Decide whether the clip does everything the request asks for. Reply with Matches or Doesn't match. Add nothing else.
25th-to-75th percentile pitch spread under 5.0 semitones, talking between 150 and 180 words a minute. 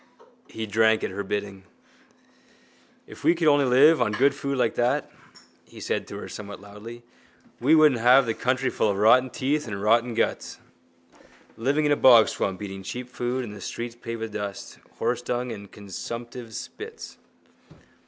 Matches